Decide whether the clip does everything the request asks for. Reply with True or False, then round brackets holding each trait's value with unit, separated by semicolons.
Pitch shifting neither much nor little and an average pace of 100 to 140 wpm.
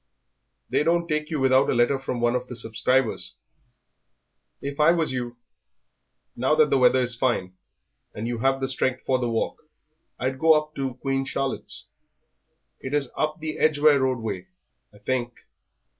False (3.3 semitones; 165 wpm)